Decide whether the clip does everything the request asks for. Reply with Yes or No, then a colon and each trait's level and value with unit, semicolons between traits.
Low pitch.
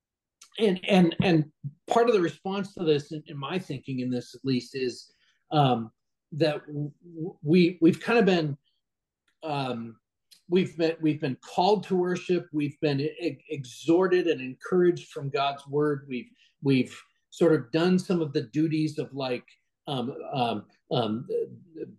No: medium, 155 Hz